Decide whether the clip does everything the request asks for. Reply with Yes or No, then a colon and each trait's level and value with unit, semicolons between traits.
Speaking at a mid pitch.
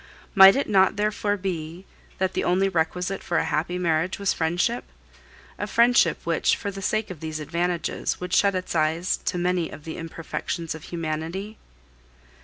Yes: medium, 180 Hz